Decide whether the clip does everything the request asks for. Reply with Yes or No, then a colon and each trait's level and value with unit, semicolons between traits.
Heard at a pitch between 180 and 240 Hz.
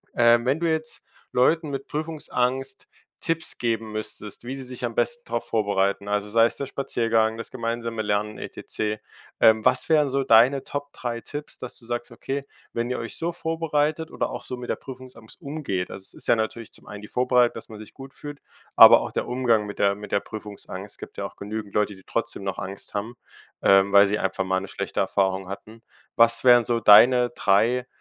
No: low, 115 Hz